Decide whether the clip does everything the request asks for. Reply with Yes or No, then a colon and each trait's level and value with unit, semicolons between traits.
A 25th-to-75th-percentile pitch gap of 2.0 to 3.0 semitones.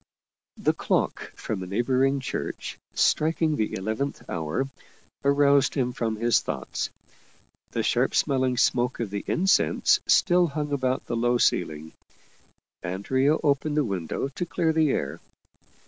No: average, 4.7 semitones